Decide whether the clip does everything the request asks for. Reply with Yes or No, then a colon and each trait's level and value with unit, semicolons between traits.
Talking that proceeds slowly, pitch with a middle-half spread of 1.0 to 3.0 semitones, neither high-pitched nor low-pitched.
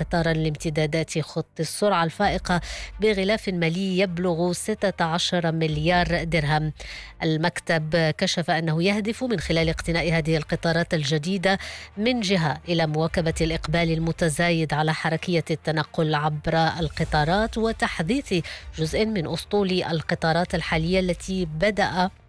Yes: slow, 105 wpm; narrow, 2.6 semitones; medium, 170 Hz